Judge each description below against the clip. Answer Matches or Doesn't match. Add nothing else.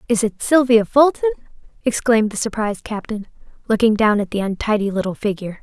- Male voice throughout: Doesn't match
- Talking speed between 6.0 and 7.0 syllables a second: Matches